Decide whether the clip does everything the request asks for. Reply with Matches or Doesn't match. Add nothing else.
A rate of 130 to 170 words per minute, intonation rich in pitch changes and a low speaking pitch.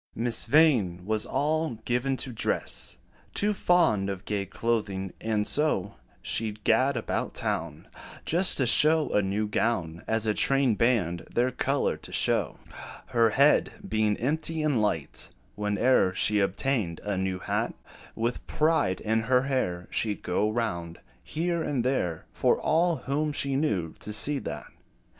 Matches